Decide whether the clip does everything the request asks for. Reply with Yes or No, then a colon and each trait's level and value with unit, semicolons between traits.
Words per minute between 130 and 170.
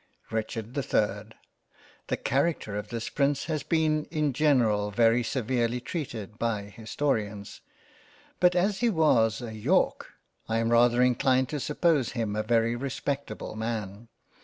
Yes: average, 140 wpm